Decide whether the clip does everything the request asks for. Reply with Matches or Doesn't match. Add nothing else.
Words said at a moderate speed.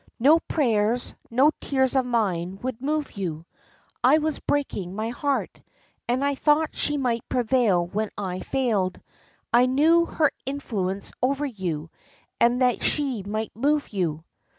Matches